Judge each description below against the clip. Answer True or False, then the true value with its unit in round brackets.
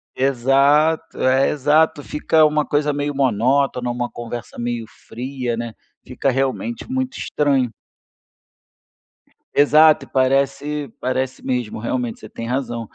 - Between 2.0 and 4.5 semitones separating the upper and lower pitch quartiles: True (3.2 semitones)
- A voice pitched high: False (135 Hz)